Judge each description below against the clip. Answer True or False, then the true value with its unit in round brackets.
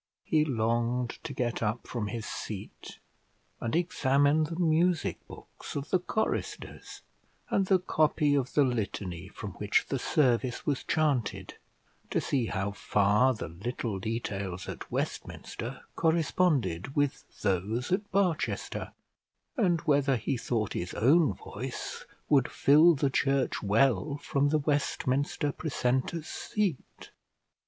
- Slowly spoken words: True (130 wpm)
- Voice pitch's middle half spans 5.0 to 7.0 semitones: True (5.5 semitones)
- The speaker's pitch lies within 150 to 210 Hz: False (135 Hz)